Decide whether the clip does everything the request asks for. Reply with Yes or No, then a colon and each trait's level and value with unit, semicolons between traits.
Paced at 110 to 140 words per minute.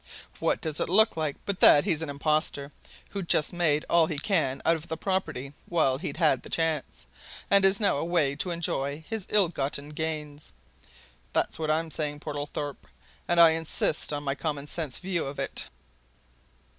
No: average, 175 wpm